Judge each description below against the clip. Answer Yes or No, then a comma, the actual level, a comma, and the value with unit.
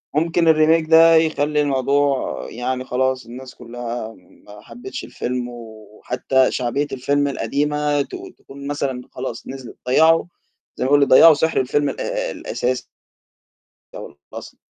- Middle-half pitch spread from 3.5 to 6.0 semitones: No, average, 3.1 semitones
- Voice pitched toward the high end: No, low, 135 Hz